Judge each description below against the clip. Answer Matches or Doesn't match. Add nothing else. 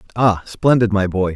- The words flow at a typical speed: Matches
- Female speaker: Doesn't match